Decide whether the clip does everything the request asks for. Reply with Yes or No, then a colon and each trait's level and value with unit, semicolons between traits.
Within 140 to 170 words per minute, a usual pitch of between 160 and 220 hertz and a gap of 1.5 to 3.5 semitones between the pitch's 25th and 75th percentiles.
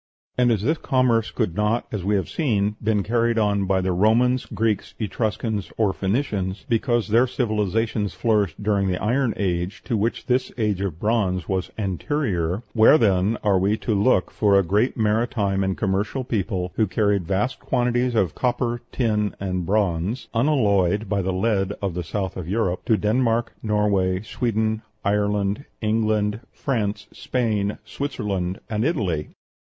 No: average, 160 wpm; low, 105 Hz; average, 3.1 semitones